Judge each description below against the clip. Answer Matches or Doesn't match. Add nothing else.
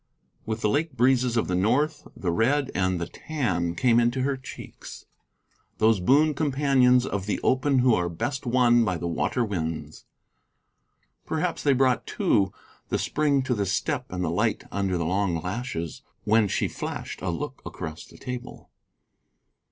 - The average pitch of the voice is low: Matches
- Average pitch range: Doesn't match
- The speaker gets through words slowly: Doesn't match